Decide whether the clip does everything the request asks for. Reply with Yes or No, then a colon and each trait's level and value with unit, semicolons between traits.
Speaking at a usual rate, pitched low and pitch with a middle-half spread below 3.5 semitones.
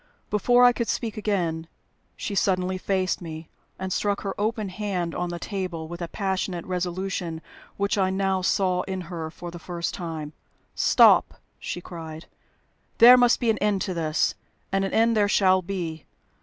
No: average, 170 wpm; medium, 185 Hz; average, 2.8 semitones